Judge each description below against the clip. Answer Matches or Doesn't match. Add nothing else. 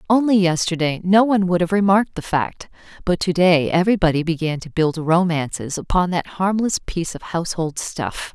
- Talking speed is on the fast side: Doesn't match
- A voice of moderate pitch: Matches